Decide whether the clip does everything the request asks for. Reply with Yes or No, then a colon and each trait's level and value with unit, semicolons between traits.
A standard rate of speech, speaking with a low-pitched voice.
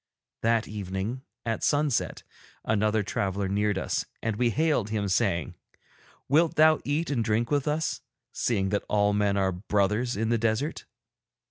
Yes: average, 150 wpm; low, 110 Hz